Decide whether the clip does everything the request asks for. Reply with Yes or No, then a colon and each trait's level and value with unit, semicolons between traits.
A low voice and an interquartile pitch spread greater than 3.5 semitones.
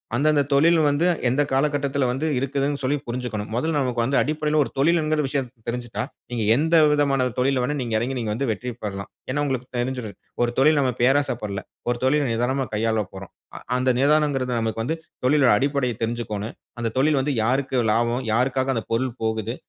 No: low, 130 Hz; average, 3.2 semitones